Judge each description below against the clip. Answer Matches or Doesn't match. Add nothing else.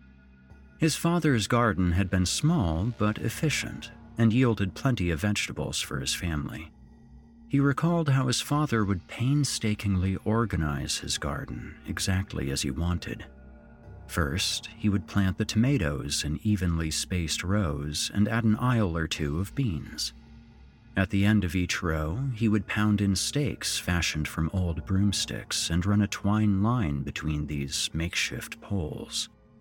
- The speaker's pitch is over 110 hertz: Doesn't match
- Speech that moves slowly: Doesn't match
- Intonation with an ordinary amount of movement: Doesn't match